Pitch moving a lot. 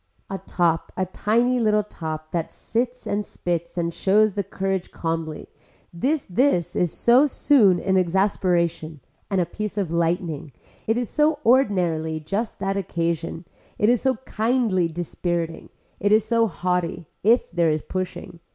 No: average, 4.3 semitones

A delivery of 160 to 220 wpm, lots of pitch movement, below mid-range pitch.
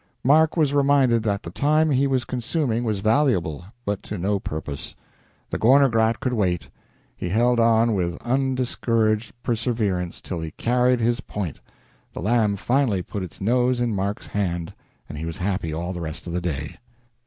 Yes: average, 175 wpm; wide, 5.7 semitones; low, 110 Hz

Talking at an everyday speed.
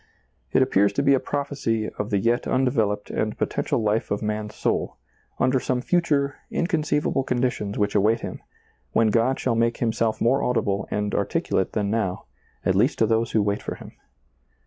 Yes: average, 175 wpm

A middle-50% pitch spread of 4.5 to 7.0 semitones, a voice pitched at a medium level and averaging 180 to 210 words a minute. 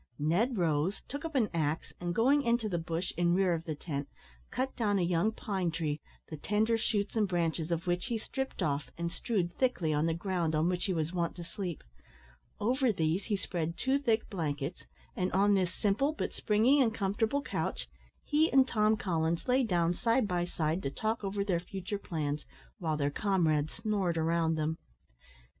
Yes: average, 4.9 semitones; medium, 180 Hz; average, 190 wpm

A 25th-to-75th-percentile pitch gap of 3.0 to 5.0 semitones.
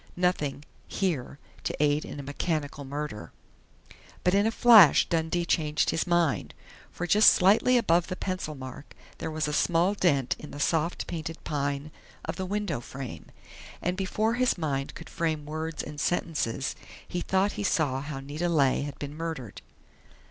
Yes: average, 3.8 semitones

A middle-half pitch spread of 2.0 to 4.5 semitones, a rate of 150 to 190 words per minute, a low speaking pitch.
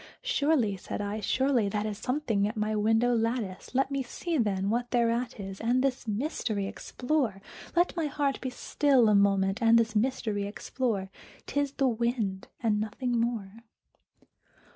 No: average, 3.9 semitones; average, 165 wpm; high, 230 Hz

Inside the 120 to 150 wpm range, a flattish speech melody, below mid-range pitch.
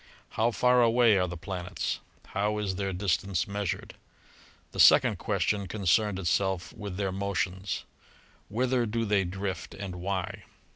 Yes: average, 140 wpm; narrow, 2.2 semitones; low, 100 Hz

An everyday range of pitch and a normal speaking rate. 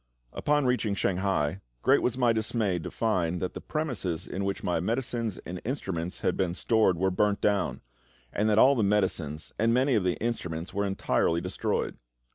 Yes: average, 4.3 semitones; average, 180 wpm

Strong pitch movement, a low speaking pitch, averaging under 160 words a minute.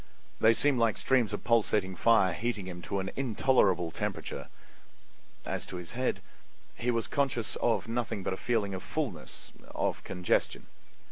No: average, 4.4 semitones; low, 110 Hz; average, 150 wpm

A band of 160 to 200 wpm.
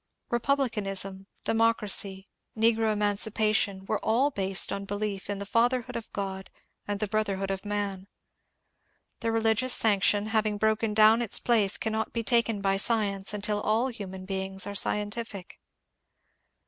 No: slow, 135 wpm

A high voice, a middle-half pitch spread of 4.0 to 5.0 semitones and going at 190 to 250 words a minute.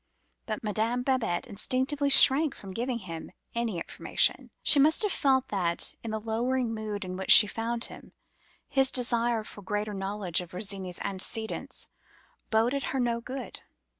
No: high, 225 Hz; average, 4.3 semitones; average, 155 wpm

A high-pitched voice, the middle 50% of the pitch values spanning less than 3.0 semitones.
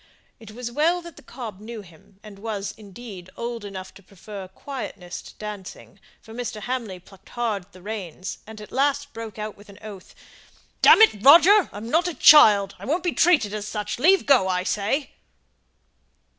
No: high, 215 Hz; average, 4.5 semitones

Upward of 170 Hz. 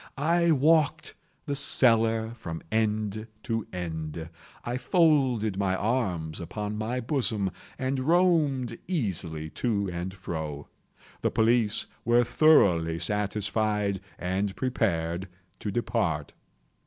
No: low, 110 Hz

